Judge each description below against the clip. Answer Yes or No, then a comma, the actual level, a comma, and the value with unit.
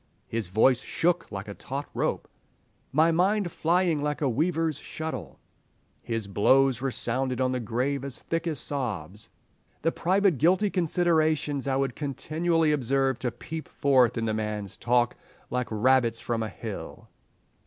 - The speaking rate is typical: Yes, average, 150 wpm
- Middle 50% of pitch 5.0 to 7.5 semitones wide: Yes, average, 5.3 semitones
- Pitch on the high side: No, low, 135 Hz